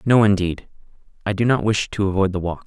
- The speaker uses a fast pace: Yes, fast, 225 wpm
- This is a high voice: No, low, 100 Hz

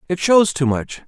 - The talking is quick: Yes, fast, 225 wpm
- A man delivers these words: Yes, male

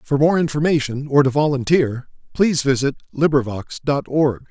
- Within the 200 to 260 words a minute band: No, average, 145 wpm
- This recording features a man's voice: Yes, male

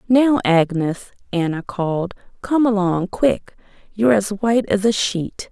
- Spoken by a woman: Yes, female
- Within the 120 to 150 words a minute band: Yes, average, 140 wpm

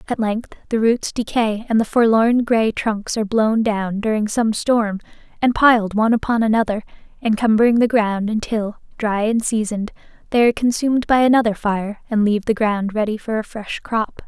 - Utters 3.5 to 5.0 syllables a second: No, 5.2 syllables/s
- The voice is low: No, high, 220 Hz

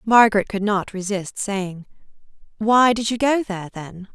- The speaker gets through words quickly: No, average, 160 wpm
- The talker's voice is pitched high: Yes, high, 205 Hz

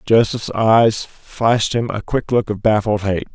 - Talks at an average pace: Yes, average, 180 wpm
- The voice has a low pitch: Yes, low, 110 Hz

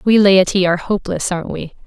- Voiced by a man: No, female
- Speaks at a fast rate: No, average, 195 wpm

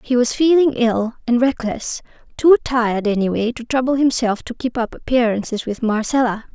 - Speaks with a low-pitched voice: No, high, 240 Hz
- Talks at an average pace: Yes, average, 165 wpm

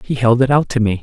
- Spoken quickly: Yes, fast, 350 wpm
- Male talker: Yes, male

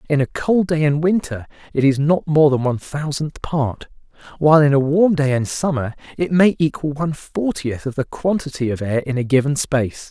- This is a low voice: No, medium, 145 Hz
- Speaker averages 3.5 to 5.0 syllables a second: No, 5.3 syllables/s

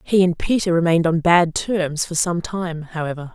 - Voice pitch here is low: No, medium, 170 Hz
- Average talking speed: Yes, average, 195 wpm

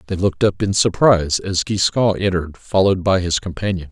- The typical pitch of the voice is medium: No, very low, 95 Hz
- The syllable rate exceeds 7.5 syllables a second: No, 5.9 syllables/s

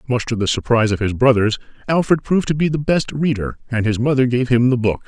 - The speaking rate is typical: No, fast, 250 wpm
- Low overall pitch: Yes, low, 125 Hz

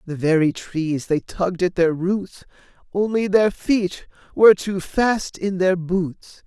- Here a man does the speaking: Yes, male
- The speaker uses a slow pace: No, average, 160 wpm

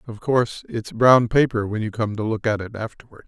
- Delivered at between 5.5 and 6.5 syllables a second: Yes, 5.6 syllables/s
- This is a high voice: No, low, 110 Hz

